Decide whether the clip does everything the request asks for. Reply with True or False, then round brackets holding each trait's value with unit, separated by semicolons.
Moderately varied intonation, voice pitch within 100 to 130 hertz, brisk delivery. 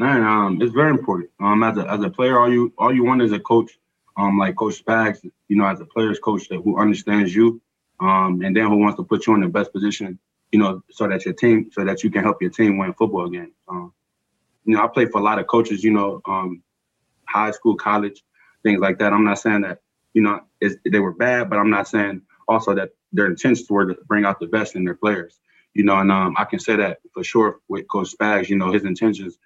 False (2.3 semitones; 105 Hz; 255 wpm)